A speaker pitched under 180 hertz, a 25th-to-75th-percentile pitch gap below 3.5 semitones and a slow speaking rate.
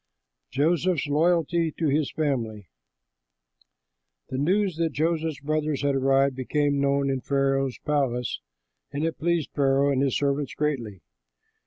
Yes: medium, 140 Hz; narrow, 2.5 semitones; slow, 130 wpm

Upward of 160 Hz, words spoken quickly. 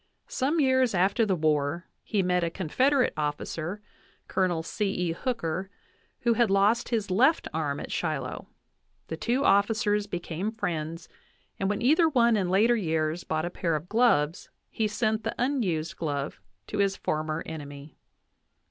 No: high, 190 Hz; average, 155 wpm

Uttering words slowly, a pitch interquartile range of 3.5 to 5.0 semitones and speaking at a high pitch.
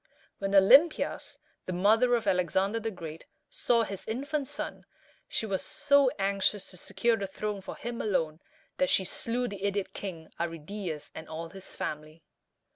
No: average, 160 wpm; average, 4.4 semitones; high, 195 Hz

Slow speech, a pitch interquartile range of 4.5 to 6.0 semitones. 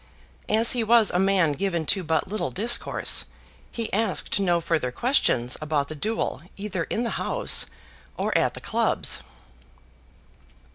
No: average, 145 wpm; wide, 5.6 semitones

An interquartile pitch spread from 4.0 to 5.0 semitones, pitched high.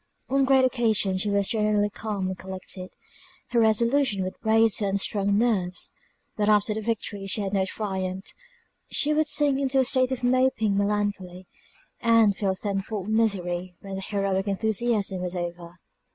No: average, 3.1 semitones; high, 205 Hz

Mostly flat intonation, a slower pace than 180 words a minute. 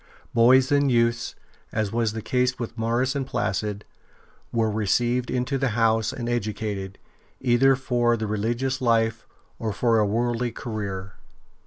Yes: narrow, 2.3 semitones; average, 145 wpm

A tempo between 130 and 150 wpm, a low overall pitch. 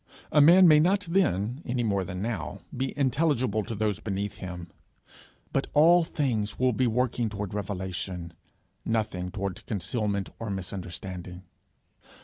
Yes: slow, 135 wpm; low, 105 Hz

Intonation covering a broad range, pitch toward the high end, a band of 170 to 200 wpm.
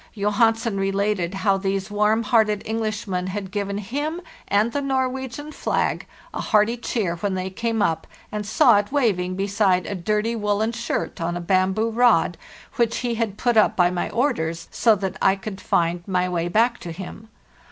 No: average, 3.3 semitones; high, 210 Hz; average, 180 wpm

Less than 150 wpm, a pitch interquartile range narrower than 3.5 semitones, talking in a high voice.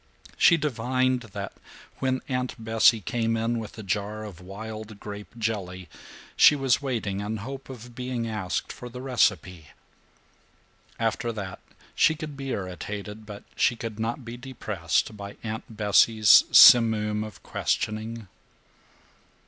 No: slow, 135 wpm; average, 3.0 semitones; low, 110 Hz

